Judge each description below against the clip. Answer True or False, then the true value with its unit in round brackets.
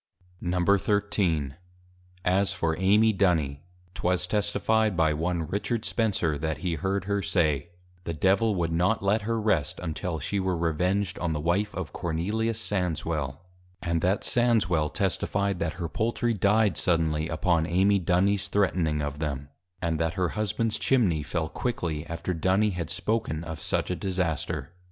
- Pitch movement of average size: True (3.9 semitones)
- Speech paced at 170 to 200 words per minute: False (150 wpm)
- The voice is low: True (90 Hz)